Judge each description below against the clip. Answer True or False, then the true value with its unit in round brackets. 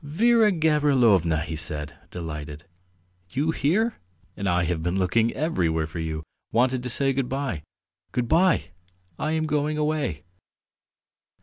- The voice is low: True (125 Hz)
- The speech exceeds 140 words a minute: False (135 wpm)